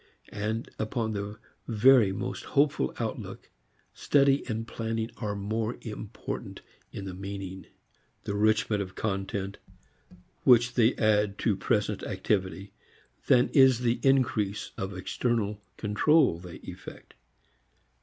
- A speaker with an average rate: No, slow, 115 wpm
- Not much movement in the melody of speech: No, average, 3.0 semitones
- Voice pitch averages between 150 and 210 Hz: No, low, 110 Hz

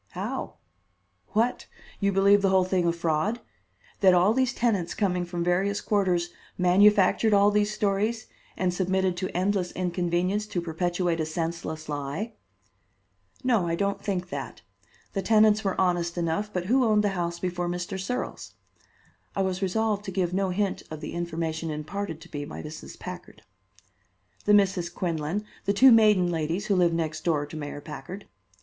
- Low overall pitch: No, medium, 185 Hz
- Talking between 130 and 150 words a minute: No, average, 165 wpm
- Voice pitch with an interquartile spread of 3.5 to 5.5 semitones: No, average, 3.0 semitones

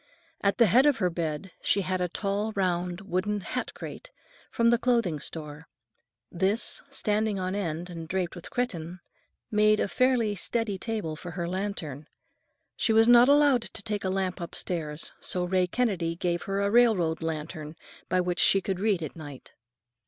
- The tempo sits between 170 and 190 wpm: Yes, average, 175 wpm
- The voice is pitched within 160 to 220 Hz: Yes, high, 190 Hz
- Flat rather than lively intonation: No, average, 4.0 semitones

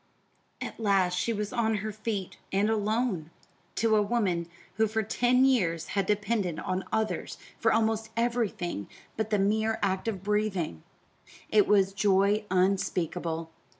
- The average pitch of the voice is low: No, high, 205 Hz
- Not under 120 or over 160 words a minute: Yes, average, 145 wpm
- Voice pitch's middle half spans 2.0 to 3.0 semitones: Yes, average, 2.7 semitones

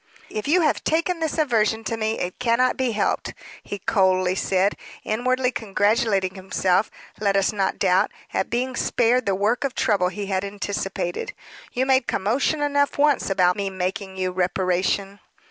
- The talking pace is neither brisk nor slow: Yes, average, 165 wpm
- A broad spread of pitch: No, average, 4.9 semitones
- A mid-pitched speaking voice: No, high, 205 Hz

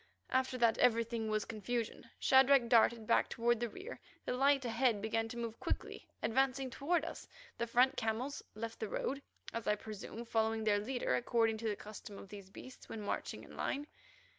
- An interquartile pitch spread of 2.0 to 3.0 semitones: Yes, average, 2.7 semitones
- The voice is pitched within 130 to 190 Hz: No, high, 230 Hz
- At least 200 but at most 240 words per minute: No, average, 185 wpm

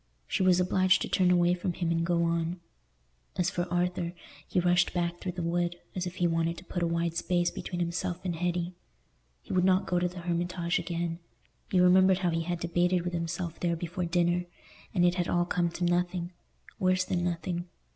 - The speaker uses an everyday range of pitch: No, narrow, 0.9 semitones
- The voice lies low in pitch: No, medium, 175 Hz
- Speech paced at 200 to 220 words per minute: Yes, fast, 205 wpm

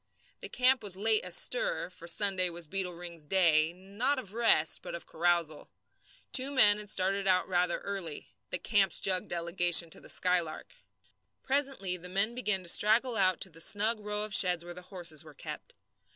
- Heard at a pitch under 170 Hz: No, medium, 185 Hz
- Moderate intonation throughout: Yes, average, 3.4 semitones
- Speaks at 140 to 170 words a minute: No, average, 180 wpm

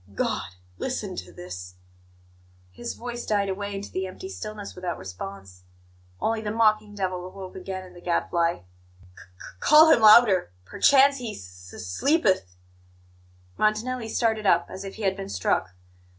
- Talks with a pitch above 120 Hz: Yes, high, 190 Hz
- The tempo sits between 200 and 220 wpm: No, average, 165 wpm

